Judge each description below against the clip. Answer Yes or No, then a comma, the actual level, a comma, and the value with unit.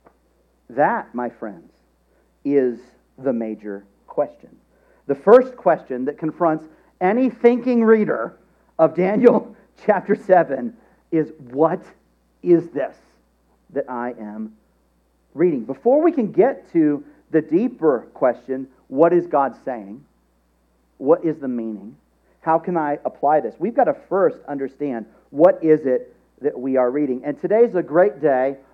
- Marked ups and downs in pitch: Yes, wide, 8.4 semitones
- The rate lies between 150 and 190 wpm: No, slow, 135 wpm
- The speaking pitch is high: No, medium, 145 Hz